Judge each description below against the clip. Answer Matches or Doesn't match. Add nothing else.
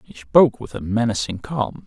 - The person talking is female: Doesn't match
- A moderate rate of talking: Matches